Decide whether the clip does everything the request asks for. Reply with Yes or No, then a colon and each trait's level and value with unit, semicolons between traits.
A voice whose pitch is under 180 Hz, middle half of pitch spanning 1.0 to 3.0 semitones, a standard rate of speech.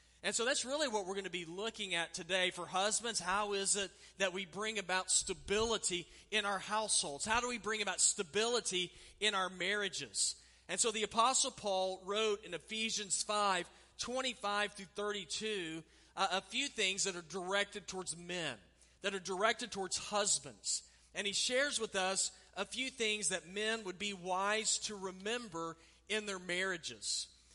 No: high, 195 Hz; average, 2.7 semitones; average, 175 wpm